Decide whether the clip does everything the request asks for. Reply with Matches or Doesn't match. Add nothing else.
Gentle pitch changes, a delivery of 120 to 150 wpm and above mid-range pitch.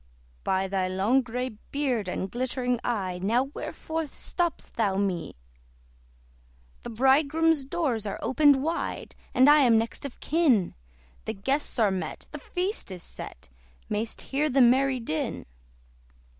Doesn't match